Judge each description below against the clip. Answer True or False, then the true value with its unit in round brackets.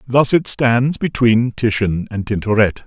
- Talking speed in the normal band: True (145 wpm)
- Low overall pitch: True (115 Hz)